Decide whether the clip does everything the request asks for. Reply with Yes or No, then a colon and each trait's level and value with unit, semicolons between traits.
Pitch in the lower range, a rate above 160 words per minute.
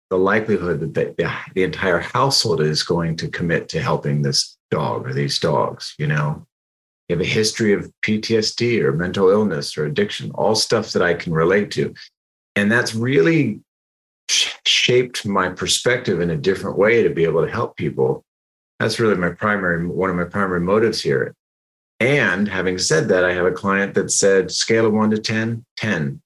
Yes: very low, 95 Hz; average, 185 wpm